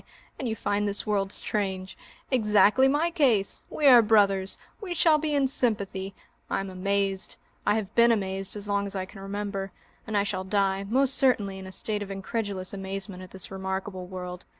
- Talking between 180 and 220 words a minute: Yes, average, 190 wpm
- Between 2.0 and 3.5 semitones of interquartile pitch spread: Yes, narrow, 2.5 semitones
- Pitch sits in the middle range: No, high, 200 Hz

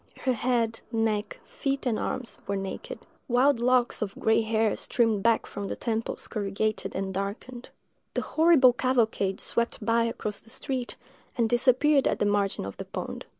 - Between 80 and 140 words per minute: No, average, 160 wpm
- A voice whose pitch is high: Yes, high, 230 Hz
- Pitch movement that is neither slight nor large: Yes, average, 3.3 semitones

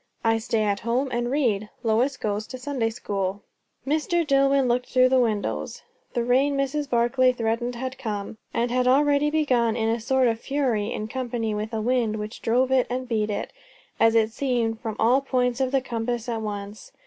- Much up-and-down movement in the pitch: No, average, 2.8 semitones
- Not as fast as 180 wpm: No, average, 195 wpm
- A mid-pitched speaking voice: No, high, 240 Hz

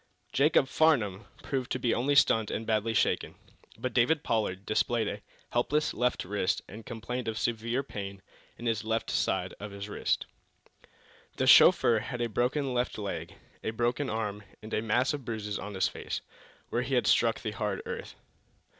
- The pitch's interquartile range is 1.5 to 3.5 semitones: Yes, average, 2.8 semitones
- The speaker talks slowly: No, average, 175 wpm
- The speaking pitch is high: No, low, 115 Hz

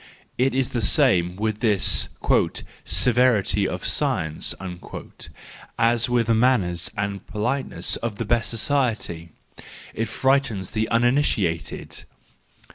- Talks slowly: Yes, slow, 110 wpm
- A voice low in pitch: Yes, low, 115 Hz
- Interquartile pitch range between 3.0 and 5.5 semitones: Yes, average, 3.8 semitones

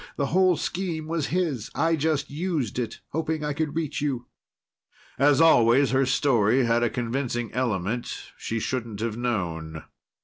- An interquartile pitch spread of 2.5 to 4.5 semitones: No, average, 5.1 semitones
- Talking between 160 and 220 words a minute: No, average, 150 wpm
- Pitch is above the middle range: No, low, 135 Hz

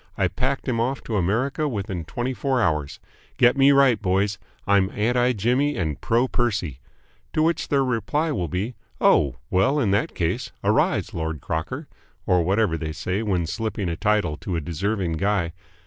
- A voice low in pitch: Yes, low, 105 Hz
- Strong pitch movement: Yes, wide, 6.2 semitones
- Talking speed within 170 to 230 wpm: Yes, average, 175 wpm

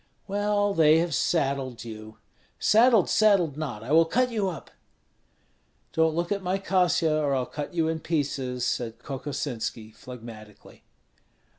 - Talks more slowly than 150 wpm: Yes, average, 140 wpm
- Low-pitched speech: No, medium, 155 Hz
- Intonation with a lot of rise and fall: Yes, wide, 6.4 semitones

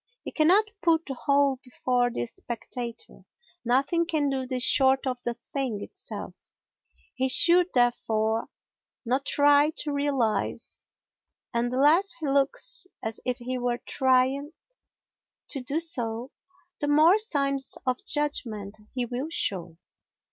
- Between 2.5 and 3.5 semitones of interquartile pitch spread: Yes, average, 3.2 semitones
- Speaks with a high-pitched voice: Yes, very high, 265 Hz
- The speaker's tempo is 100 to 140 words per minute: Yes, slow, 135 wpm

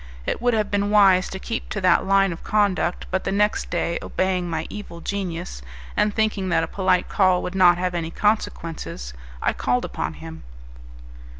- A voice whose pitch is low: No, medium, 185 Hz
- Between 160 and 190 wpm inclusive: Yes, average, 185 wpm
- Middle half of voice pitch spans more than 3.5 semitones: No, average, 2.8 semitones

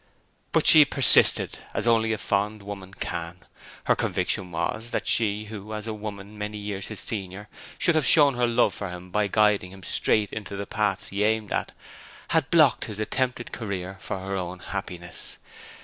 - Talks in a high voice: No, low, 105 Hz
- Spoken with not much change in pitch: Yes, narrow, 2.2 semitones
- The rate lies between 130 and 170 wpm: No, average, 180 wpm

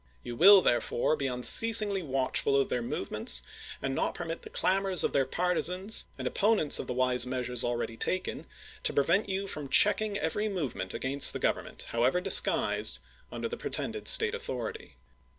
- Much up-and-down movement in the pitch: Yes, wide, 7.8 semitones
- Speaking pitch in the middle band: Yes, medium, 160 Hz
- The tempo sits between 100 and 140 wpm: No, average, 170 wpm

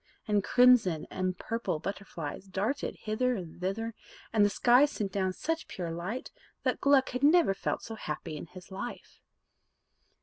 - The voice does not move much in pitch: No, average, 5.2 semitones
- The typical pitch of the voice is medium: No, high, 205 Hz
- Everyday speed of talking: Yes, average, 160 wpm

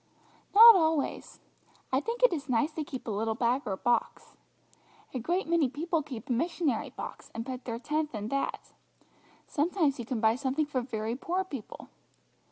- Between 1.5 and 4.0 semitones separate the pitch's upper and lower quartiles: No, average, 5.3 semitones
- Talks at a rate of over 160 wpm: Yes, average, 175 wpm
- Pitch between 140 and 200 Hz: No, very high, 275 Hz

